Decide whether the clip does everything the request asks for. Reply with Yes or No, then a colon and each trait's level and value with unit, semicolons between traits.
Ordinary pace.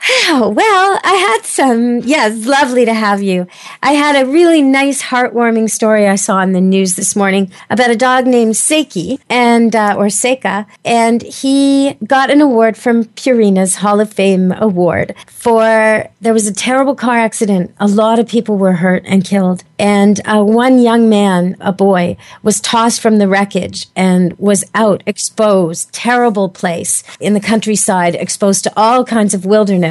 Yes: average, 175 wpm